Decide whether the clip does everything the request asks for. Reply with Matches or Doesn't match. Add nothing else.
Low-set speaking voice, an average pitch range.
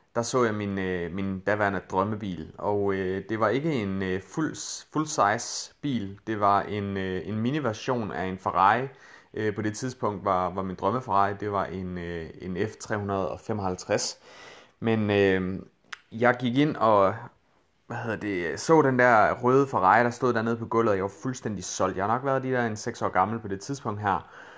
Matches